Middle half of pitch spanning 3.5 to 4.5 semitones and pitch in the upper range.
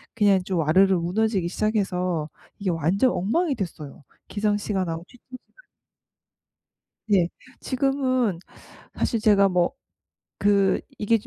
Yes: average, 3.8 semitones; high, 195 Hz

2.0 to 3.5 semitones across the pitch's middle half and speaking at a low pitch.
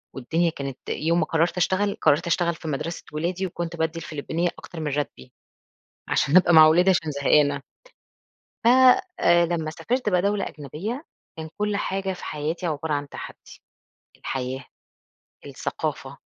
No: average, 3.0 semitones; medium, 165 Hz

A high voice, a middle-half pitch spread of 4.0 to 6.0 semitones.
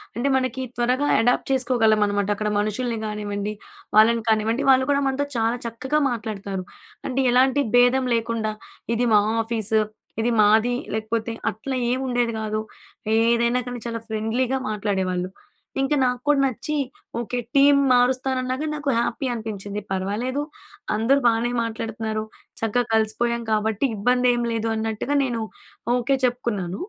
No: high, 235 Hz; average, 2.8 semitones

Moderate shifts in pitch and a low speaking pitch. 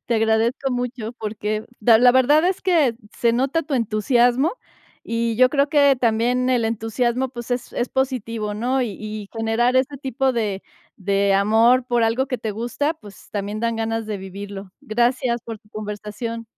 No: average, 3.0 semitones; high, 235 Hz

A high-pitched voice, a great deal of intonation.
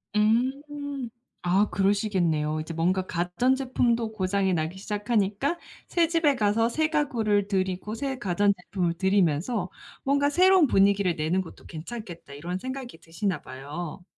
Yes: high, 200 Hz; wide, 5.9 semitones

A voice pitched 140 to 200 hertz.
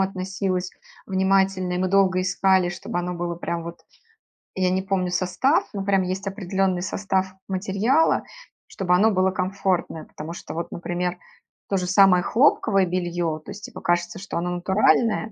Yes: medium, 185 Hz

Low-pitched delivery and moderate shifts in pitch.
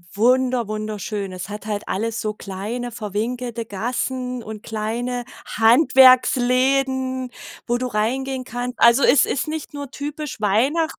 No: high, 245 Hz; average, 3.2 semitones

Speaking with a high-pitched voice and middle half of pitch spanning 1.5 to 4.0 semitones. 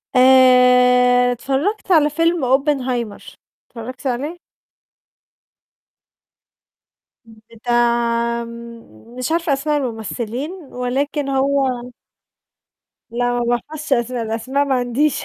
Yes: very high, 255 Hz; average, 2.9 semitones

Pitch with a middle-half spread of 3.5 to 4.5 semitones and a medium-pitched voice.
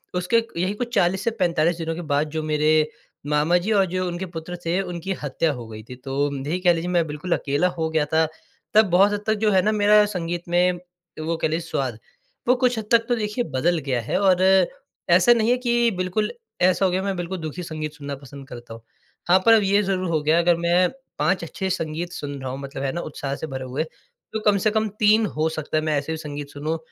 Yes: average, 4.2 semitones; medium, 170 Hz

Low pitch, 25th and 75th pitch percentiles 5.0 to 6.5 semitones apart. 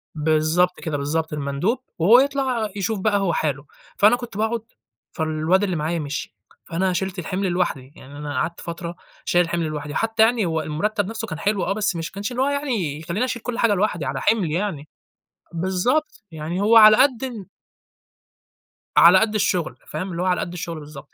No: medium, 180 Hz; average, 5.3 semitones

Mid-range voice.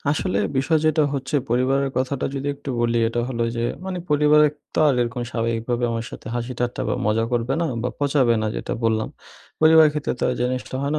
No: low, 130 Hz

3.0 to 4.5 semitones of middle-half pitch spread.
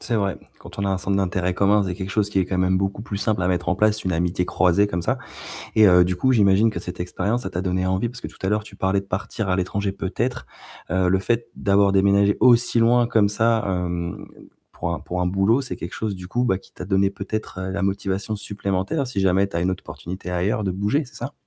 No: narrow, 2.4 semitones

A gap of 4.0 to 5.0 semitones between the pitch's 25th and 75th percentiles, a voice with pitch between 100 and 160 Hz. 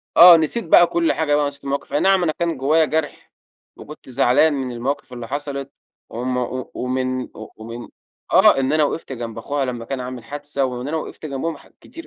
No: average, 3.5 semitones; medium, 140 Hz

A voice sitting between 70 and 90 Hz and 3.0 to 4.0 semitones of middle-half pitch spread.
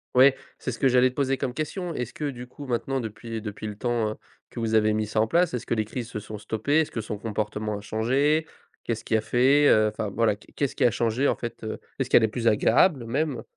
No: low, 115 Hz; average, 3.6 semitones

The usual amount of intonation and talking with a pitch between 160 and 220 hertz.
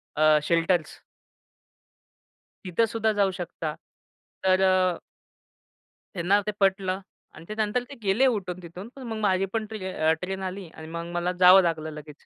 Yes: average, 3.0 semitones; medium, 185 Hz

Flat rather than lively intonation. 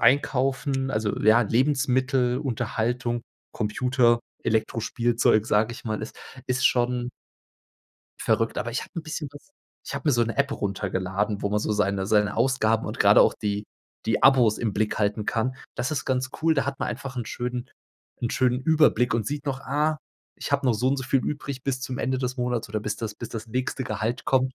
No: average, 3.2 semitones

